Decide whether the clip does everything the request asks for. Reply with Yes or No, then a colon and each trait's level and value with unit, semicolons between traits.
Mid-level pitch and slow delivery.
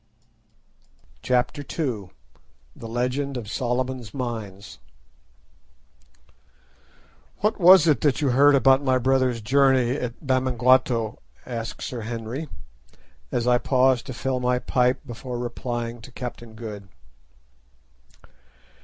No: low, 125 Hz; slow, 110 wpm